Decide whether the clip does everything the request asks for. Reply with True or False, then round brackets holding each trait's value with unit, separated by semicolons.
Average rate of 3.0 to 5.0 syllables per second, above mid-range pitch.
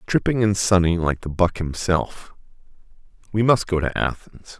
False (4.6 syllables/s; 95 Hz)